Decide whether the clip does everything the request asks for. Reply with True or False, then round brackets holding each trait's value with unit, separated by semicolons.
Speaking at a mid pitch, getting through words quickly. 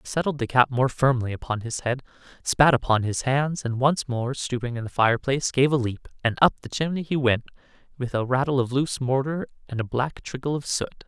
False (130 Hz; 220 wpm)